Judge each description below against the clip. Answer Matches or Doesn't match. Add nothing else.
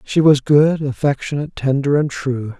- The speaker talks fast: Doesn't match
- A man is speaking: Matches